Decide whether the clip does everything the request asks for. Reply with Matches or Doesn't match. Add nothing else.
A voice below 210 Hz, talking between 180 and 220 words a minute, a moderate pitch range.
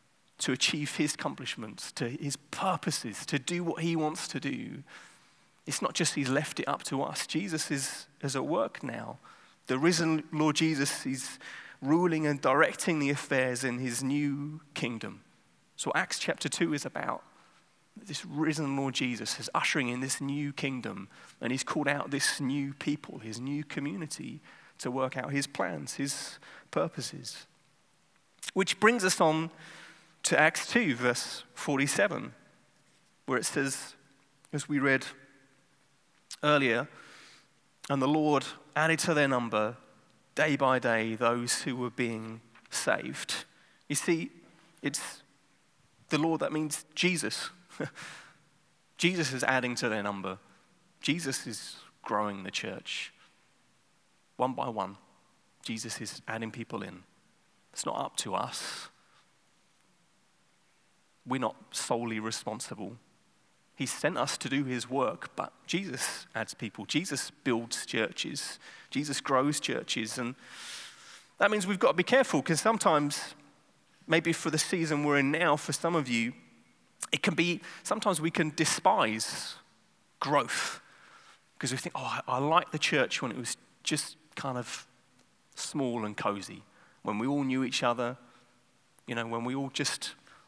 Doesn't match